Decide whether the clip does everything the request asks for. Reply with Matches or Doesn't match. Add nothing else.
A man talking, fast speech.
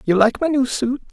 Matches